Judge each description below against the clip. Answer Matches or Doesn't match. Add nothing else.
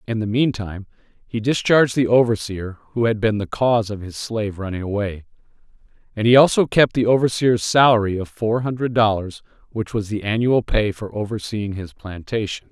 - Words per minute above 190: Doesn't match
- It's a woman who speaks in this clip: Doesn't match